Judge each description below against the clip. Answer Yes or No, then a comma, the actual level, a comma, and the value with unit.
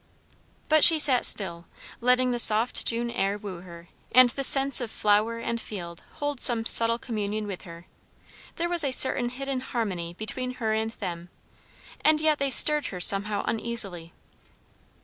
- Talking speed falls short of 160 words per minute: No, average, 165 wpm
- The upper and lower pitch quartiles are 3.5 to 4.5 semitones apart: Yes, average, 4.2 semitones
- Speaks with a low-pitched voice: No, high, 230 Hz